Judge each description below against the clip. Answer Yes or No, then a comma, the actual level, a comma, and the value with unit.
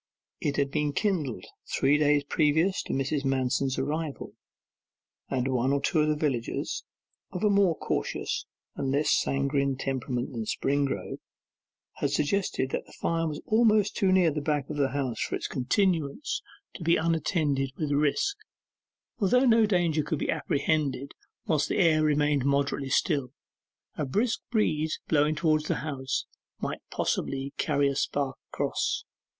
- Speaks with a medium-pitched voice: Yes, medium, 145 Hz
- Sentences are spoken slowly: No, average, 150 wpm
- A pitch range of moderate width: Yes, average, 3.0 semitones